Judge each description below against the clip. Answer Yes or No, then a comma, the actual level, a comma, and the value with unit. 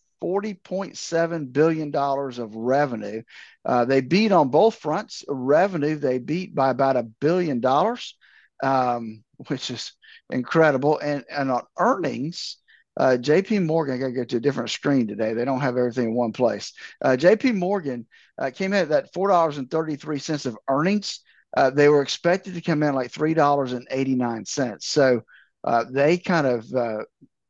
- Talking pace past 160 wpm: Yes, average, 170 wpm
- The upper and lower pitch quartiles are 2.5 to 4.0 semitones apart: No, average, 4.9 semitones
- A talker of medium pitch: Yes, medium, 145 Hz